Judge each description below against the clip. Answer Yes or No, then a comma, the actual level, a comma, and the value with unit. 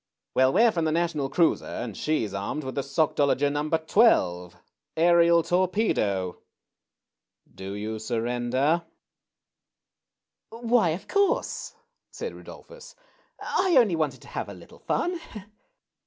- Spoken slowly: Yes, slow, 130 wpm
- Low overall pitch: No, medium, 155 Hz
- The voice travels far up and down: Yes, wide, 7.4 semitones